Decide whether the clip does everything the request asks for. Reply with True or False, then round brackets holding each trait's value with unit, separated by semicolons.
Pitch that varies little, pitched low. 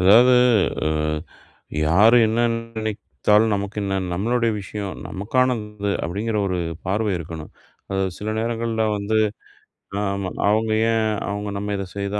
True (2.1 semitones; 105 Hz)